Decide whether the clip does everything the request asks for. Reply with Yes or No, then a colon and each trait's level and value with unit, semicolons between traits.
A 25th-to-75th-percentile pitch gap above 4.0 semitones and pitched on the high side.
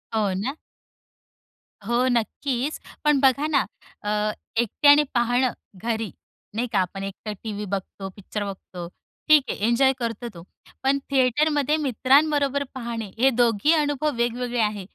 Yes: average, 4.8 semitones; high, 240 Hz